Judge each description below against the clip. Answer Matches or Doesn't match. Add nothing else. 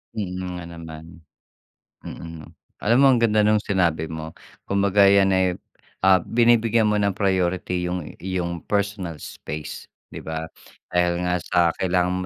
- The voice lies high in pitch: Doesn't match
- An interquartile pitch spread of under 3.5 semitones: Matches